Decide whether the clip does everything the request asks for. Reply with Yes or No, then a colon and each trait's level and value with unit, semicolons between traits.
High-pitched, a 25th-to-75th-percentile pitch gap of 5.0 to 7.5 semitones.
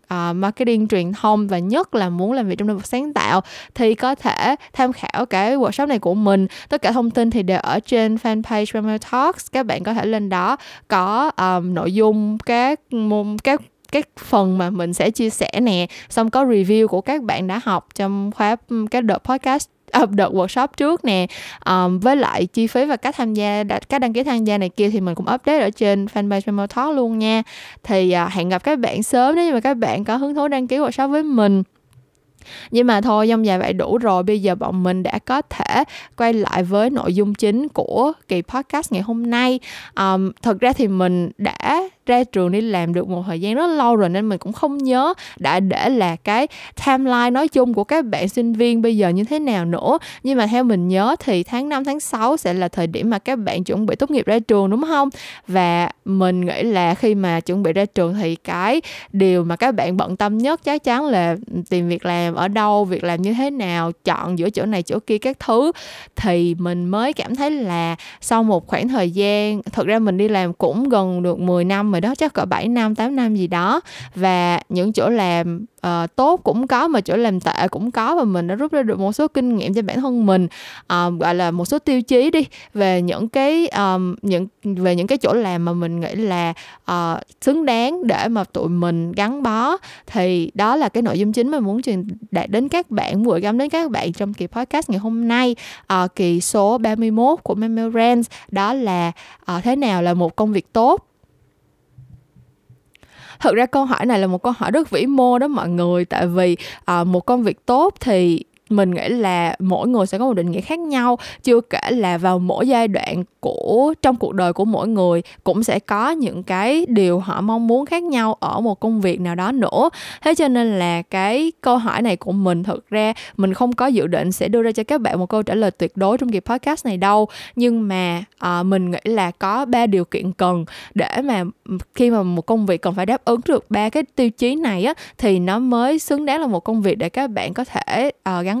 Yes: high, 215 Hz; average, 5.3 semitones